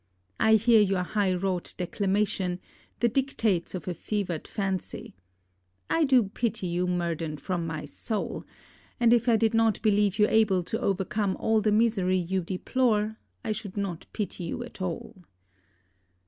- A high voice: Yes, high, 200 Hz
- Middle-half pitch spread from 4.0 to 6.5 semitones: No, average, 3.4 semitones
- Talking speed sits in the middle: Yes, average, 155 wpm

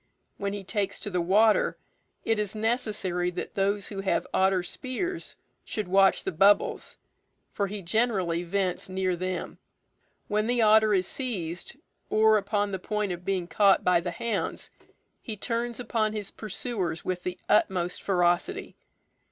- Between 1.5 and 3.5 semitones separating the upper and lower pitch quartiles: Yes, average, 3.0 semitones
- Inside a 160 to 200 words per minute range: No, average, 150 wpm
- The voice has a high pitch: Yes, high, 200 Hz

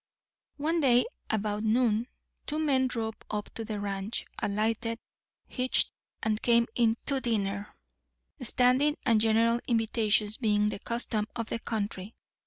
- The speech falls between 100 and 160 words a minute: Yes, slow, 135 wpm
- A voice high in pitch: Yes, high, 225 Hz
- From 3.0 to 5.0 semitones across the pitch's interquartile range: No, narrow, 2.6 semitones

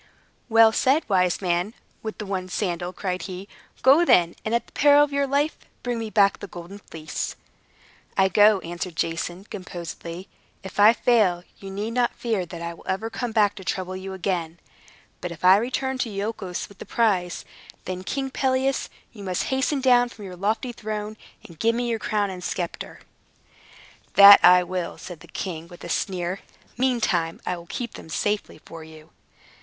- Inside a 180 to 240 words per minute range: Yes, average, 185 wpm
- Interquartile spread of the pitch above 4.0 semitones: Yes, average, 4.4 semitones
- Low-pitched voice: No, high, 195 Hz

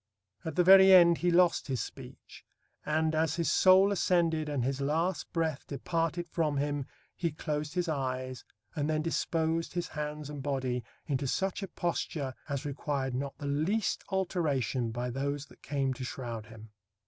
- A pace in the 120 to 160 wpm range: No, average, 170 wpm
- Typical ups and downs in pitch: Yes, average, 3.9 semitones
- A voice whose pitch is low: No, medium, 150 Hz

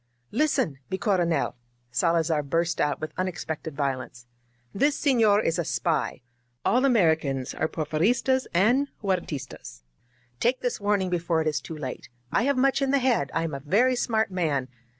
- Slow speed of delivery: No, average, 170 wpm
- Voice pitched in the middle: Yes, medium, 170 Hz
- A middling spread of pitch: No, wide, 7.3 semitones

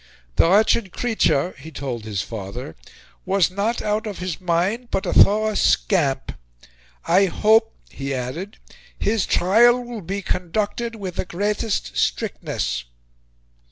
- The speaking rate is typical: No, slow, 130 wpm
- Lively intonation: Yes, wide, 6.7 semitones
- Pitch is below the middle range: No, high, 190 Hz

